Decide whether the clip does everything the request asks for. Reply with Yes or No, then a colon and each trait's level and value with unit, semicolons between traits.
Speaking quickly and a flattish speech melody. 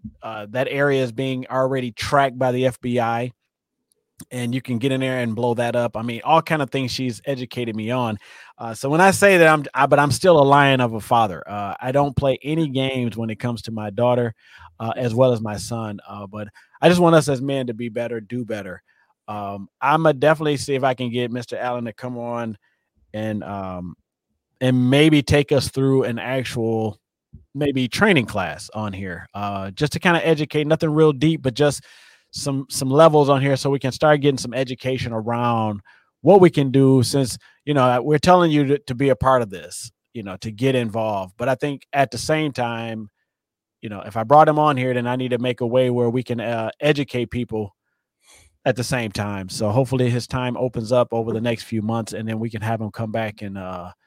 No: fast, 225 wpm; average, 3.5 semitones